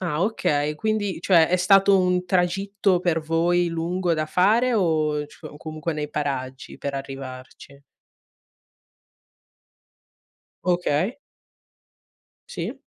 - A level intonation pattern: No, average, 3.8 semitones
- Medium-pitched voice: Yes, medium, 170 Hz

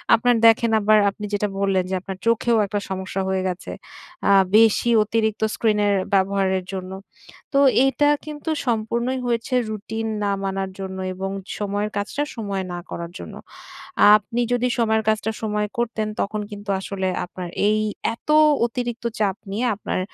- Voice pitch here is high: Yes, high, 210 Hz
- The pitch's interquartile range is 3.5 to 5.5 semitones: No, average, 2.9 semitones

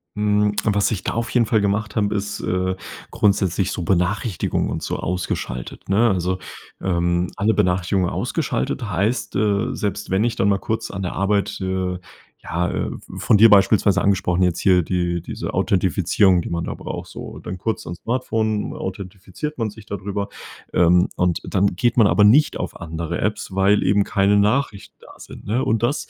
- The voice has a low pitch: Yes, low, 100 Hz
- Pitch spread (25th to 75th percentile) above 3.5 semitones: No, narrow, 2.6 semitones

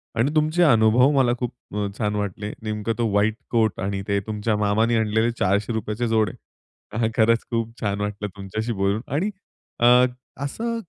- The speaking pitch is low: Yes, low, 110 Hz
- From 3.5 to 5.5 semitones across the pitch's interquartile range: No, narrow, 2.4 semitones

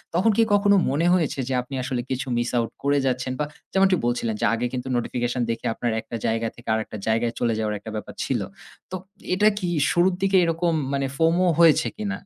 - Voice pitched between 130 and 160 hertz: Yes, low, 135 Hz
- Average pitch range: No, wide, 6.8 semitones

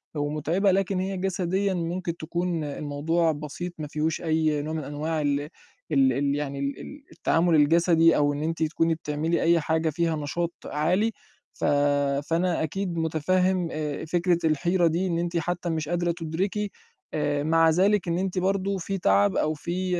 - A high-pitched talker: No, medium, 165 Hz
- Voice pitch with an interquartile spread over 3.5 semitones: No, average, 2.8 semitones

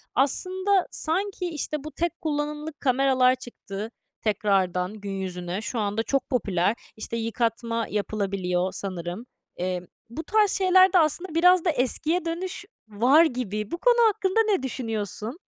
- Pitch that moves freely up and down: Yes, wide, 8.4 semitones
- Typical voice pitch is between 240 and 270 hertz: Yes, very high, 250 Hz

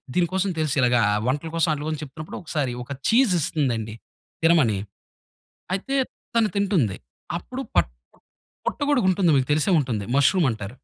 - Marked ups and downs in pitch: Yes, wide, 6.9 semitones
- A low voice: No, medium, 155 Hz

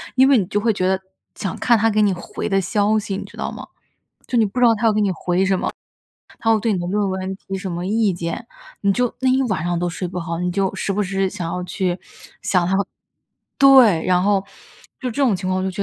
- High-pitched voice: Yes, high, 195 Hz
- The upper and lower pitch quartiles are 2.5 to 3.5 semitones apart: Yes, average, 3.1 semitones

